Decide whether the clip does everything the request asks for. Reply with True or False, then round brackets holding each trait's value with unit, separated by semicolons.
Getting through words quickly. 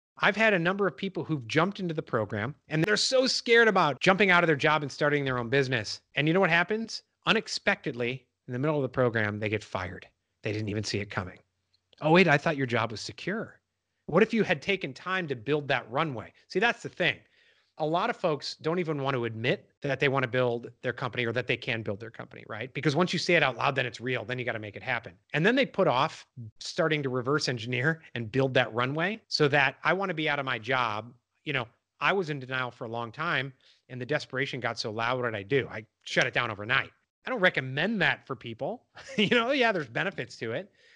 True (250 wpm)